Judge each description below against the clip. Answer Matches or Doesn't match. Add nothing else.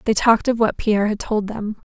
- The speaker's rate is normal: Doesn't match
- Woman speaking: Matches